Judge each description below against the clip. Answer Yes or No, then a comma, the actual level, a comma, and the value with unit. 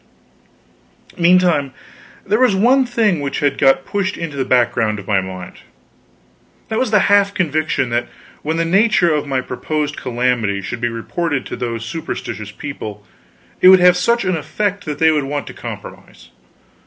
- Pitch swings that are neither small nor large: No, wide, 7.1 semitones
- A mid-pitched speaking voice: Yes, medium, 150 Hz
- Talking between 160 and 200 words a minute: Yes, average, 165 wpm